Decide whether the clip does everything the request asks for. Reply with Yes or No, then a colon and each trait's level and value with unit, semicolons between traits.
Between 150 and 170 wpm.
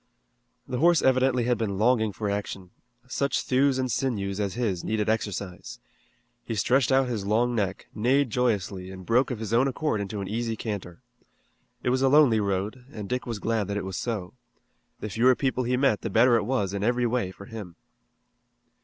No: average, 195 wpm